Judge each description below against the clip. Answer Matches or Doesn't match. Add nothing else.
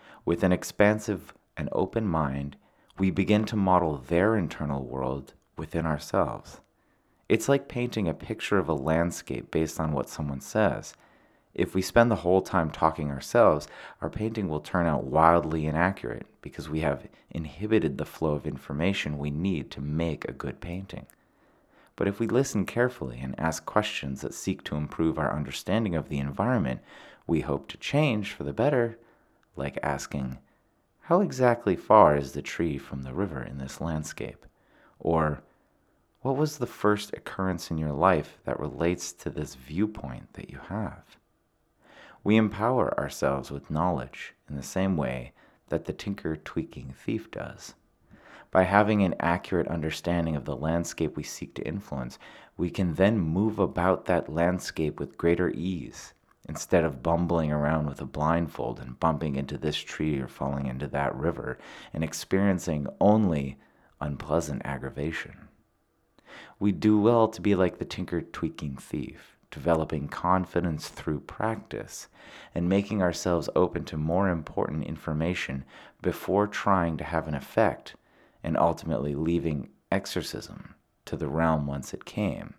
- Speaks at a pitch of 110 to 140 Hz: Doesn't match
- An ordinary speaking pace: Matches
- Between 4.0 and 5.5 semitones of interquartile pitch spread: Matches